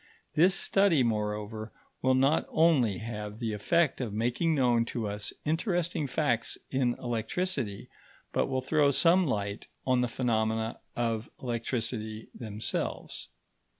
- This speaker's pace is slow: Yes, slow, 125 wpm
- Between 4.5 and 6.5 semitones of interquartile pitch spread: Yes, average, 4.9 semitones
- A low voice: Yes, low, 120 Hz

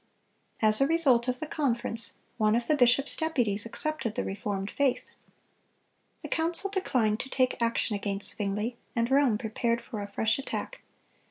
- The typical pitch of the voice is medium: No, high, 235 Hz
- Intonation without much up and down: No, average, 4.4 semitones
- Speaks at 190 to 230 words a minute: No, average, 165 wpm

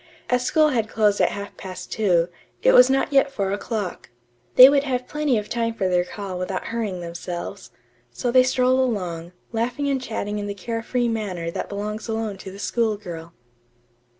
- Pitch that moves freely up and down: No, average, 4.7 semitones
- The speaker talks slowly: No, average, 190 wpm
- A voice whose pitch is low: No, high, 215 Hz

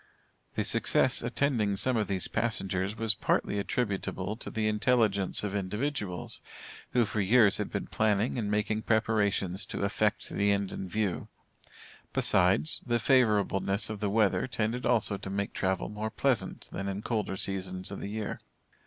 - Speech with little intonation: Yes, narrow, 2.3 semitones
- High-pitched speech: No, low, 105 Hz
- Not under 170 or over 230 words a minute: No, average, 160 wpm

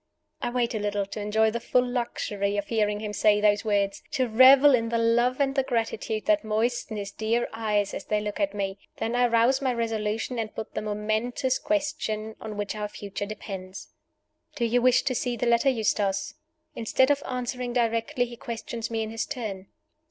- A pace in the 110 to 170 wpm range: No, average, 195 wpm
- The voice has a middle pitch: No, high, 225 Hz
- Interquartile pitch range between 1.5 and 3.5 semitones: Yes, average, 2.8 semitones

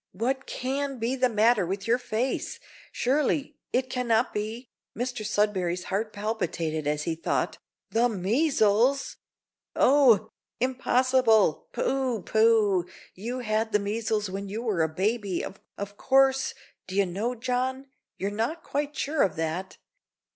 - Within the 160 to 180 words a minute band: No, slow, 135 wpm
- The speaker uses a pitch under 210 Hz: No, high, 225 Hz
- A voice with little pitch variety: No, average, 4.3 semitones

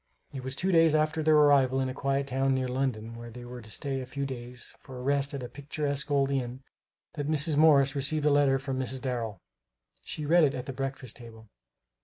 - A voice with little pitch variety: Yes, narrow, 2.2 semitones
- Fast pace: Yes, fast, 220 wpm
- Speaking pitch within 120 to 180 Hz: Yes, low, 135 Hz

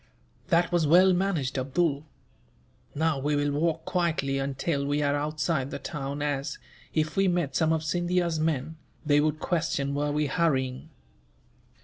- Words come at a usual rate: Yes, average, 150 wpm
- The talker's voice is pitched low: No, medium, 150 Hz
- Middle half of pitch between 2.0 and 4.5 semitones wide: Yes, average, 3.0 semitones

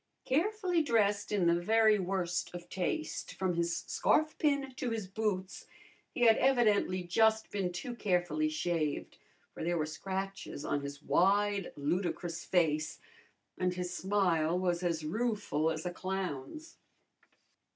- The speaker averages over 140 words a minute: No, slow, 135 wpm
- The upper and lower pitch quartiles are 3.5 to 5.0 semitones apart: Yes, average, 4.3 semitones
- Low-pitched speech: No, medium, 185 Hz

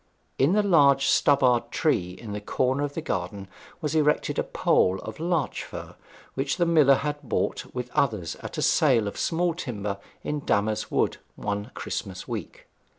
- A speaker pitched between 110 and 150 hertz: Yes, low, 135 Hz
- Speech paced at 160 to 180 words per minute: Yes, average, 170 wpm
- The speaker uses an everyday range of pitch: No, wide, 6.5 semitones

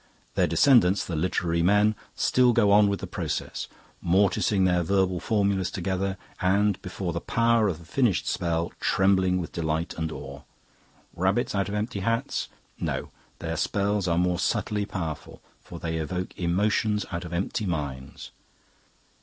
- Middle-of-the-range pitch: No, very low, 95 Hz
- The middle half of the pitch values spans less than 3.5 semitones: Yes, average, 3.1 semitones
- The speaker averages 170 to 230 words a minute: No, average, 155 wpm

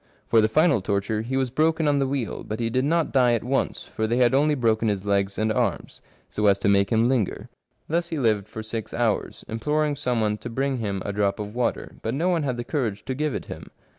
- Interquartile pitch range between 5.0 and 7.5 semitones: No, average, 4.3 semitones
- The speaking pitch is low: Yes, low, 120 Hz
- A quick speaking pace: Yes, fast, 250 wpm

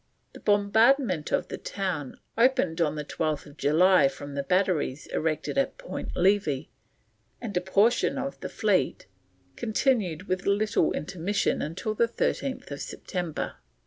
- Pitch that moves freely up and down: Yes, wide, 5.8 semitones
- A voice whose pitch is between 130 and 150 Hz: No, medium, 185 Hz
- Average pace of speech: No, slow, 130 wpm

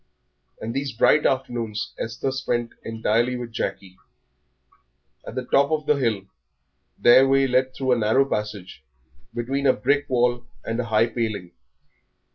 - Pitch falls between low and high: No, low, 120 Hz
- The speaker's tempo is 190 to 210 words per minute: No, average, 145 wpm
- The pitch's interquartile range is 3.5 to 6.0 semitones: No, average, 3.1 semitones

